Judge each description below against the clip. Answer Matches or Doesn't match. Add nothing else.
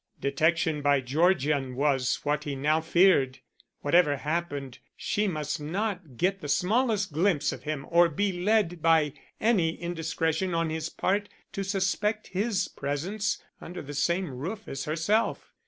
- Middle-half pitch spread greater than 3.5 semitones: Matches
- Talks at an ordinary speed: Matches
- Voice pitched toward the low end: Doesn't match